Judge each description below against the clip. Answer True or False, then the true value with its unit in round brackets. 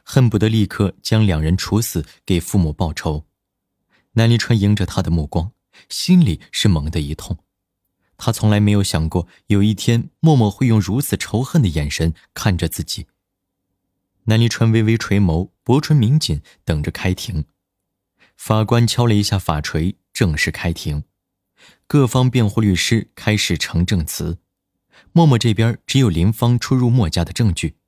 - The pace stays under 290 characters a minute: True (235 characters per minute)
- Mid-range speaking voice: False (100 Hz)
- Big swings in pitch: False (4.7 semitones)